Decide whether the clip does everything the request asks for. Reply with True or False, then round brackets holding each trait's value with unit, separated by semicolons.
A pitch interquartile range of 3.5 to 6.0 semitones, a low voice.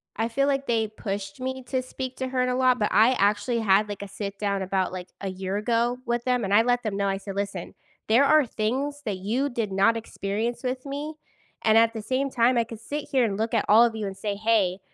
False (4.0 semitones; 225 Hz)